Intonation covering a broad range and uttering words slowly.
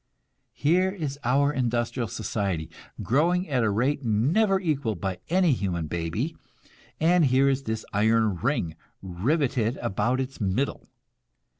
Yes: wide, 5.9 semitones; slow, 130 wpm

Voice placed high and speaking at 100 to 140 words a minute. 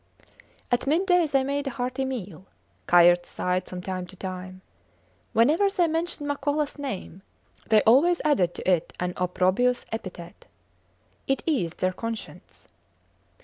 Yes: high, 230 Hz; slow, 135 wpm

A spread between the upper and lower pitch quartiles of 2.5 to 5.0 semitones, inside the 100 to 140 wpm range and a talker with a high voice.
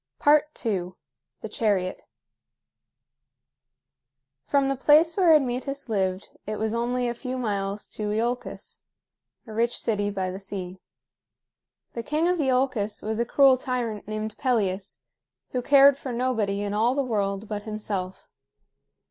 Yes: average, 4.1 semitones; slow, 135 wpm; high, 225 Hz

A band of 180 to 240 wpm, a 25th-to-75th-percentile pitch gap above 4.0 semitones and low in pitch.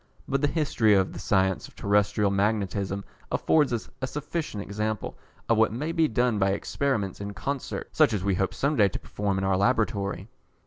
Yes: average, 190 wpm; average, 4.7 semitones; low, 105 Hz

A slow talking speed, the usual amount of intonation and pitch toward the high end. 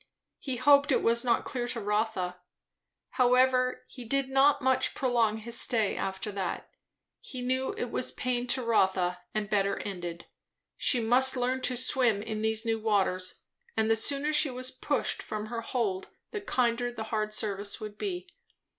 No: average, 170 wpm; average, 3.2 semitones; high, 235 Hz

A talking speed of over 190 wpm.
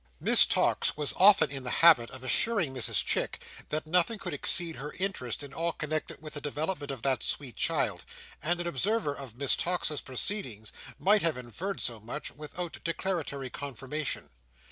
No: average, 170 wpm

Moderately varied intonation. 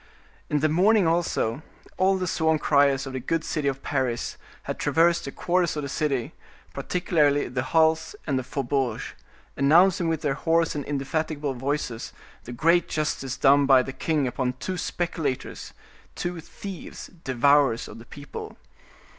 Yes: average, 3.5 semitones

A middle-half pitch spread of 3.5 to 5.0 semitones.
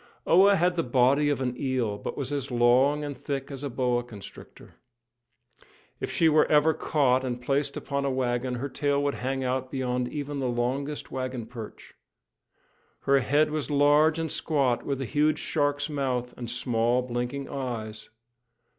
No: average, 2.7 semitones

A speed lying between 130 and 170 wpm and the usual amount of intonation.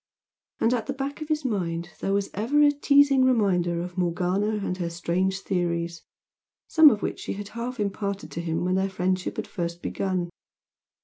No: average, 185 wpm; average, 5.0 semitones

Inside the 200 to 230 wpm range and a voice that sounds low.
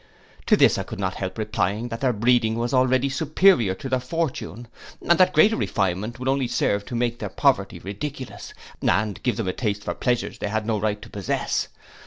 Yes: fast, 205 wpm; low, 120 Hz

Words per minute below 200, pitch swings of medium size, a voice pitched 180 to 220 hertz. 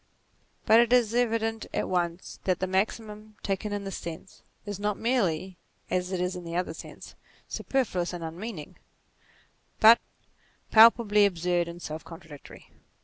Yes: average, 145 wpm; average, 4.1 semitones; high, 190 Hz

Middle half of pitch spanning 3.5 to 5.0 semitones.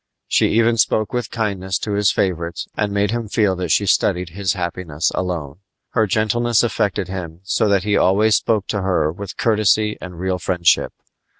No: average, 2.9 semitones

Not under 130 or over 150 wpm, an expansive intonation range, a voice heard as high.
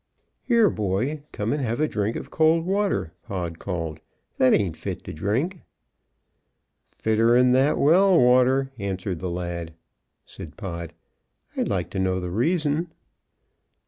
No: average, 140 wpm; wide, 8.6 semitones; low, 115 Hz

